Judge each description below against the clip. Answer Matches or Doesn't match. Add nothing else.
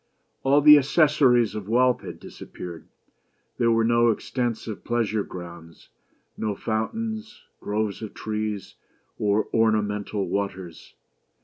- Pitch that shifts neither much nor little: Matches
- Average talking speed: Doesn't match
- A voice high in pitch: Doesn't match